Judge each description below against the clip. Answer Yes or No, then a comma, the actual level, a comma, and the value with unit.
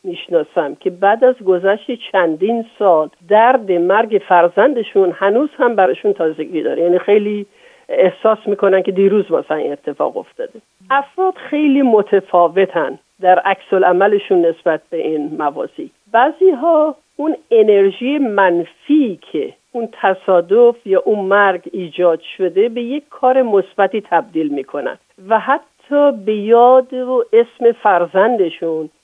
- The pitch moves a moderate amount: No, wide, 5.7 semitones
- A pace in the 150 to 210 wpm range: No, average, 125 wpm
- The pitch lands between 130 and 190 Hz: No, high, 205 Hz